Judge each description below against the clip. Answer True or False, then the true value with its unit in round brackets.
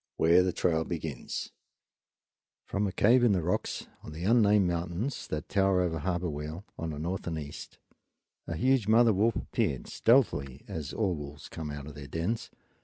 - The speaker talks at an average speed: True (180 wpm)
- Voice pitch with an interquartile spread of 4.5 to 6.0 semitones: True (4.8 semitones)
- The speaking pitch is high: False (85 Hz)